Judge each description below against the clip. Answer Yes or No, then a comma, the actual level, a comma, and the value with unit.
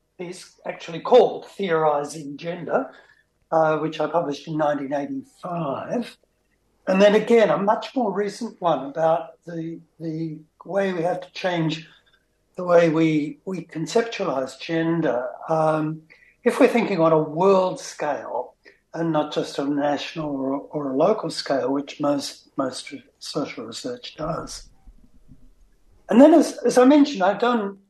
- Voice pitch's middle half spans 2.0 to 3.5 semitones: No, average, 4.3 semitones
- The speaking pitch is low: No, medium, 165 Hz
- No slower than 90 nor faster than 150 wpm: Yes, average, 140 wpm